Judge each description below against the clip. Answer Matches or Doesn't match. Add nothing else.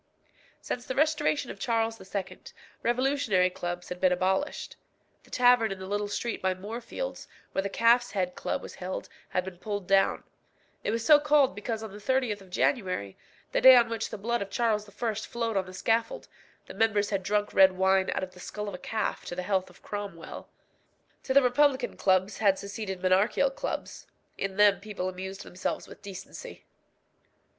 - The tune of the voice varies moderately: Matches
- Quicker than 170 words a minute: Matches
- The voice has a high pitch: Matches